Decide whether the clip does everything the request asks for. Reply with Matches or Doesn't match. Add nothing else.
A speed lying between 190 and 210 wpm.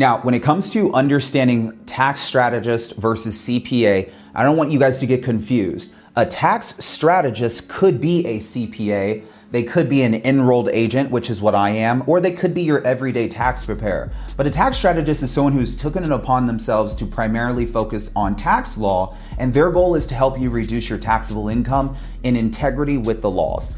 Matches